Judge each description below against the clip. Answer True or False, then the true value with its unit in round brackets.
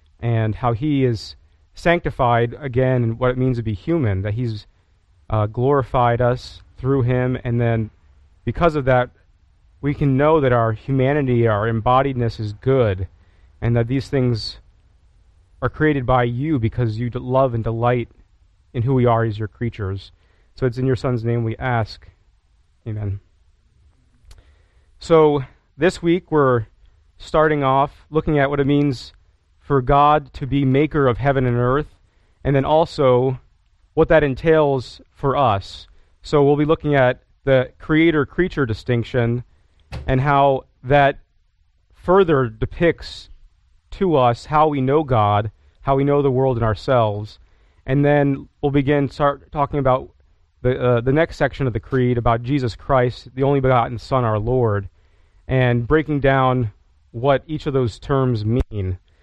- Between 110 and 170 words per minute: True (155 wpm)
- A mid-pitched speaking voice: False (125 Hz)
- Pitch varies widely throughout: True (5.8 semitones)